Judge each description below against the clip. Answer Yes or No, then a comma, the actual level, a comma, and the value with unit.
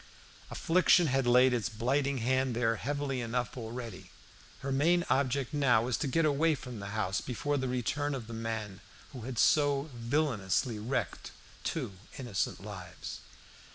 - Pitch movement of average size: Yes, average, 3.7 semitones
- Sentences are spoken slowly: No, average, 155 wpm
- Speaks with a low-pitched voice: Yes, low, 125 Hz